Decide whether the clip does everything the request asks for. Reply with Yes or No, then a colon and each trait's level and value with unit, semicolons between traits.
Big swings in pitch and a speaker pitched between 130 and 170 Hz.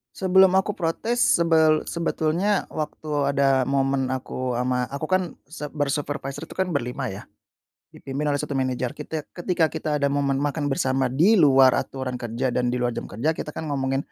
No: average, 3.3 semitones; medium, 140 Hz